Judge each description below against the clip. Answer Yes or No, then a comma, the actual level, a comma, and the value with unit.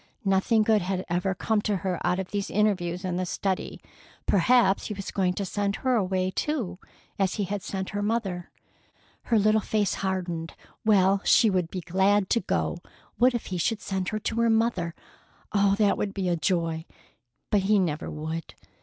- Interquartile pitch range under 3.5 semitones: Yes, average, 2.7 semitones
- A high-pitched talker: Yes, high, 195 Hz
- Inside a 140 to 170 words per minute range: No, average, 180 wpm